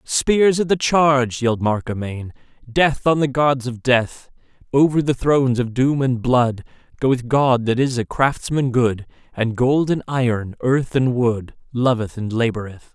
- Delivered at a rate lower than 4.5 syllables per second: Yes, 4.2 syllables/s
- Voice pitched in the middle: No, low, 125 Hz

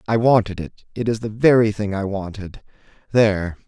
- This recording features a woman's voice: No, male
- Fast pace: No, average, 165 wpm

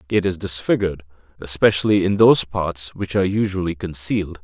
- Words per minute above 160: No, average, 150 wpm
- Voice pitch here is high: No, very low, 90 Hz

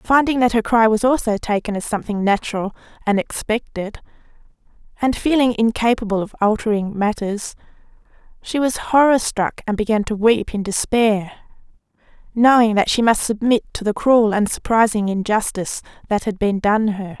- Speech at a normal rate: Yes, average, 155 wpm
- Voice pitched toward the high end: Yes, high, 220 Hz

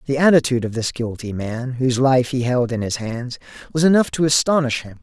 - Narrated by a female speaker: No, male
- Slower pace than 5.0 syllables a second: No, 5.7 syllables/s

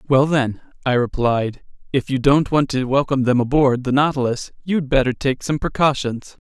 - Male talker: Yes, male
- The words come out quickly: No, average, 175 wpm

